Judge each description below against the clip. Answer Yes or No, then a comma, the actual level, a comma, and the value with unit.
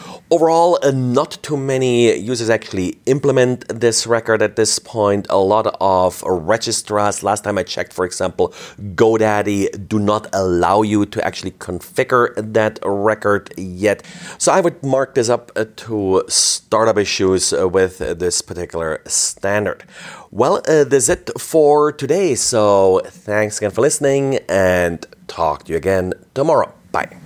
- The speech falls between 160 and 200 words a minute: No, average, 145 wpm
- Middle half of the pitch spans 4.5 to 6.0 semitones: Yes, average, 4.9 semitones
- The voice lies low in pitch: Yes, low, 105 Hz